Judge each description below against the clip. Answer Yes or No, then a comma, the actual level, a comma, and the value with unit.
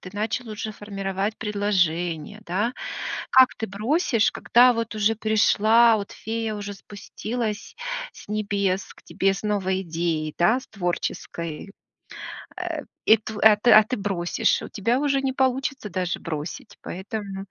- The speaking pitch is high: Yes, high, 210 Hz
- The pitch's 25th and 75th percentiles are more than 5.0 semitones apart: No, average, 2.8 semitones